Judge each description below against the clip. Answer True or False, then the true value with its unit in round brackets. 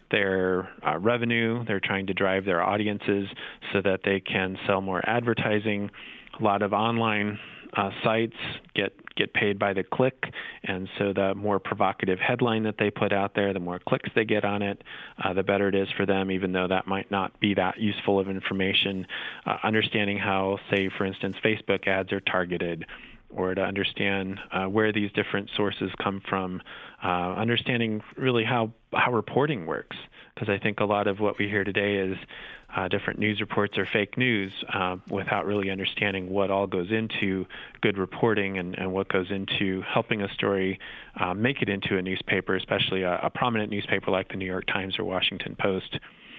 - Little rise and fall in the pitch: True (1.9 semitones)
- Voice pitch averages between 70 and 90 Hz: False (100 Hz)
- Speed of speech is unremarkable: True (190 wpm)